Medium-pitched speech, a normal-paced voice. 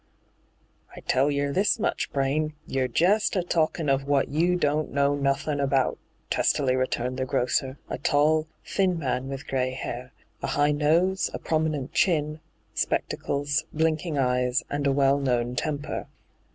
Yes: medium, 145 Hz; average, 160 wpm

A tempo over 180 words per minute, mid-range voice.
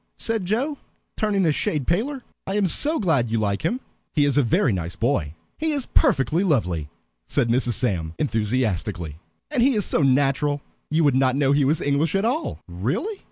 Yes: average, 190 wpm; medium, 145 Hz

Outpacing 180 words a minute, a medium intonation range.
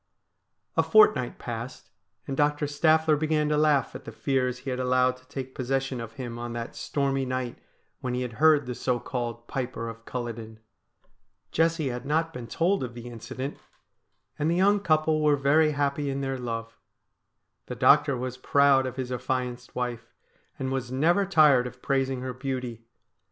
No: average, 175 wpm; average, 3.1 semitones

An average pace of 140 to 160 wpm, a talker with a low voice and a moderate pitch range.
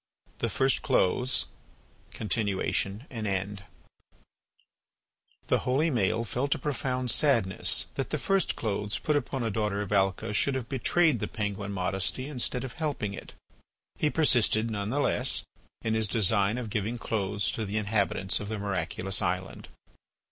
Yes: average, 150 wpm; low, 110 Hz; average, 4.2 semitones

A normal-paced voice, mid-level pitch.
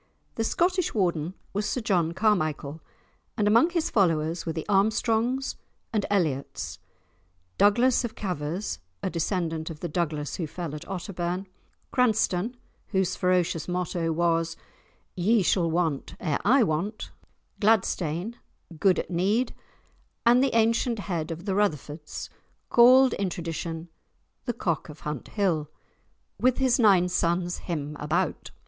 No: slow, 130 wpm; medium, 180 Hz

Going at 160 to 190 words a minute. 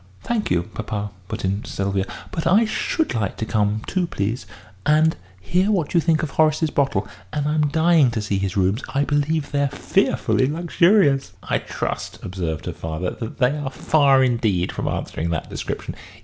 Yes: average, 175 wpm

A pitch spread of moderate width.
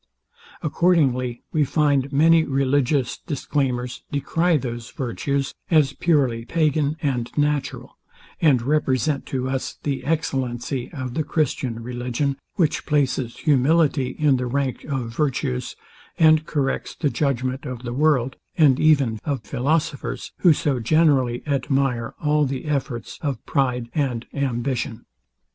Yes: average, 3.2 semitones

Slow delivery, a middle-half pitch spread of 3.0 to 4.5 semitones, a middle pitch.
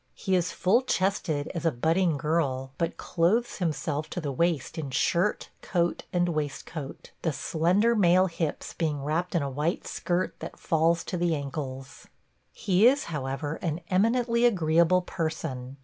No: average, 155 wpm; average, 3.5 semitones; medium, 165 Hz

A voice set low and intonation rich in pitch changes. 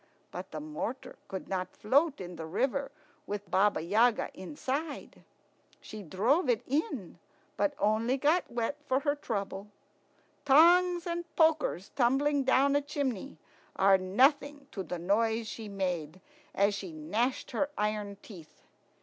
No: high, 235 Hz; wide, 6.6 semitones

